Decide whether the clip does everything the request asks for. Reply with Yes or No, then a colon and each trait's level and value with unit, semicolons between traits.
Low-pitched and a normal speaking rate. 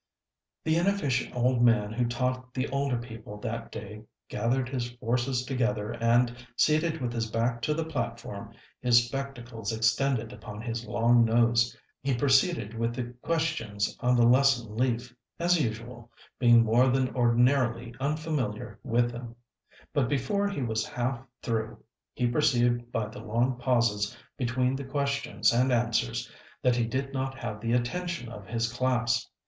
Yes: low, 120 Hz; average, 155 wpm